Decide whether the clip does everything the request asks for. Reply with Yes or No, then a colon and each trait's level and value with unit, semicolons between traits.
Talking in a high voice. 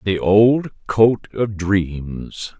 No: low, 100 Hz